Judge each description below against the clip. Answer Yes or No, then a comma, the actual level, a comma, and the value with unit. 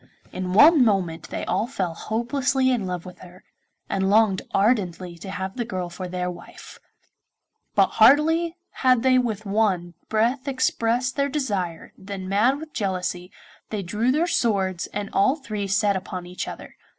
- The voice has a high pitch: Yes, high, 205 Hz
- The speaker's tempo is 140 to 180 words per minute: Yes, average, 165 wpm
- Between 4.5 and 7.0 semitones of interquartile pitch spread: Yes, wide, 5.4 semitones